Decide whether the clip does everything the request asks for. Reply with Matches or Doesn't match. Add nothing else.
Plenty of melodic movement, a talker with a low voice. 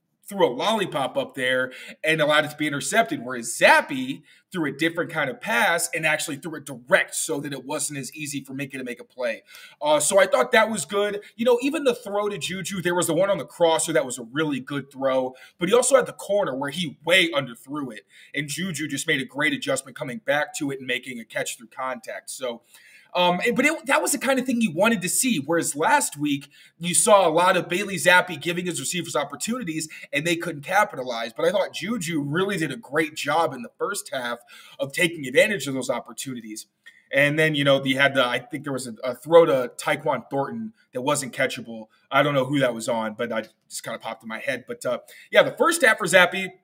Doesn't match